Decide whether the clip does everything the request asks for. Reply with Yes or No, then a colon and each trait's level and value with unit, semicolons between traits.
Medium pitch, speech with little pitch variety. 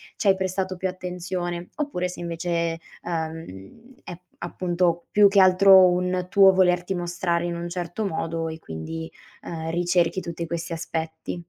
Yes: medium, 175 Hz; narrow, 1.8 semitones